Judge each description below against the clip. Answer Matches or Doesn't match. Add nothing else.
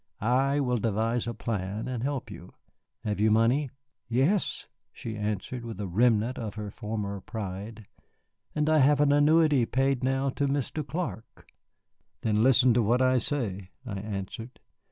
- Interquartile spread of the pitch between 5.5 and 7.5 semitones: Doesn't match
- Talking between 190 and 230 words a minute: Doesn't match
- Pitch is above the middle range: Doesn't match